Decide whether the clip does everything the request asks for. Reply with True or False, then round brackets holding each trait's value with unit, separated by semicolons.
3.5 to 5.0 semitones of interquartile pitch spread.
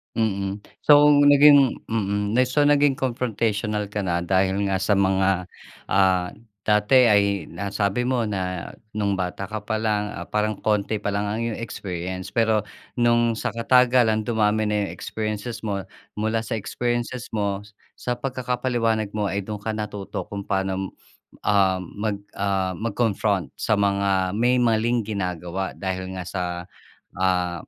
False (3.0 semitones)